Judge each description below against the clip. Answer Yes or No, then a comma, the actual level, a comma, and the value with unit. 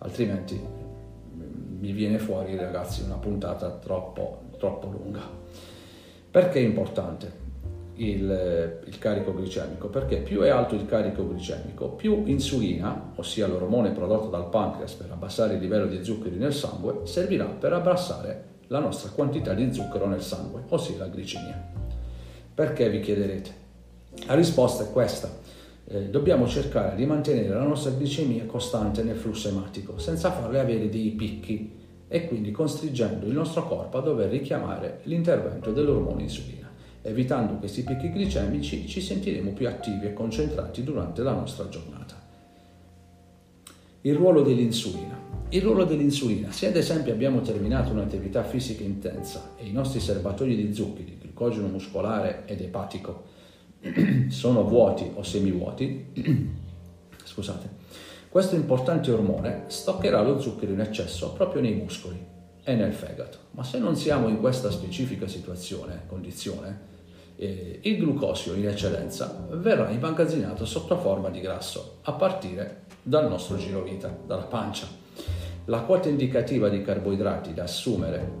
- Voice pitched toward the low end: Yes, low, 100 Hz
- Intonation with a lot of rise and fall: Yes, wide, 5.8 semitones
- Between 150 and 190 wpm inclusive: No, average, 140 wpm